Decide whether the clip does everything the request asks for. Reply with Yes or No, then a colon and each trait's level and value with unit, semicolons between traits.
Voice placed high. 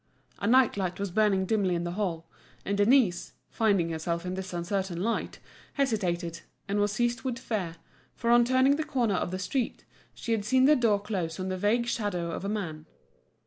Yes: high, 200 Hz